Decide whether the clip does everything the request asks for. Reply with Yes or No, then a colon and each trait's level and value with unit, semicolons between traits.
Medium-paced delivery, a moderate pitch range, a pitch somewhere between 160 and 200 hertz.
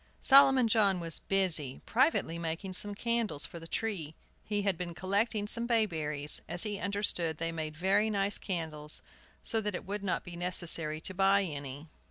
Yes: average, 175 wpm; average, 4.2 semitones; high, 190 Hz